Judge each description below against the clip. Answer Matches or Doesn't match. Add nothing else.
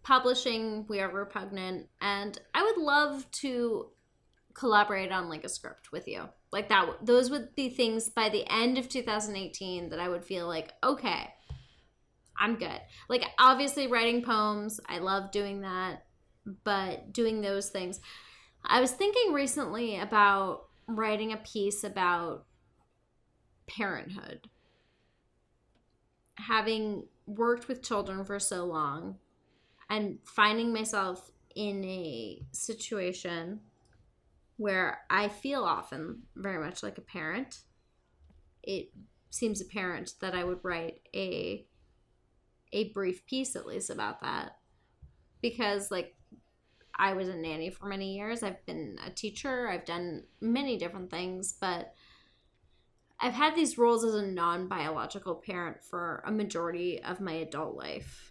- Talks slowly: Matches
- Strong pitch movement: Doesn't match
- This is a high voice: Matches